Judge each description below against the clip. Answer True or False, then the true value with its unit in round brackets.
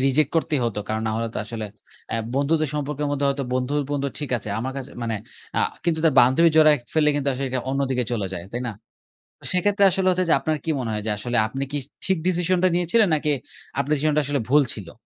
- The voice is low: False (145 Hz)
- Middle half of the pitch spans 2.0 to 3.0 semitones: False (4.0 semitones)